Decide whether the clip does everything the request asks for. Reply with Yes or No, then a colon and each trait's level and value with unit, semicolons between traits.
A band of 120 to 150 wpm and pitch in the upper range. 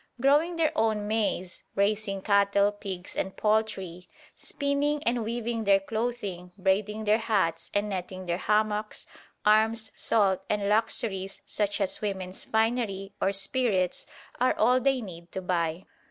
Yes: average, 140 wpm; high, 210 Hz